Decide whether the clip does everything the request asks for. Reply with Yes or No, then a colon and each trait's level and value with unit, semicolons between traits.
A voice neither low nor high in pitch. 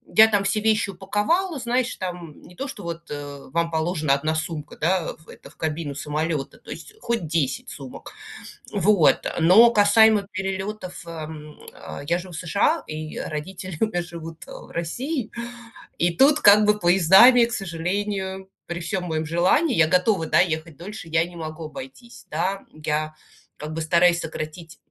Yes: medium, 175 Hz